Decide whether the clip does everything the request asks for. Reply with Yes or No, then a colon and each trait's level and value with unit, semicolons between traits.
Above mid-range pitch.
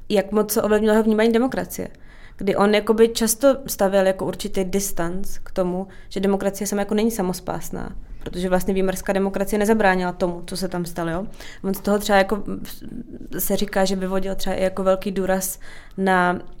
Yes: high, 195 Hz